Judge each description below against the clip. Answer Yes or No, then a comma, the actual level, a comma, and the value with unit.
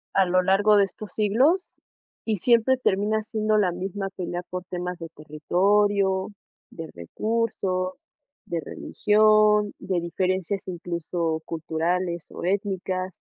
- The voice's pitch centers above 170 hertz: Yes, high, 190 Hz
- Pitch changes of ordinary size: Yes, average, 3.0 semitones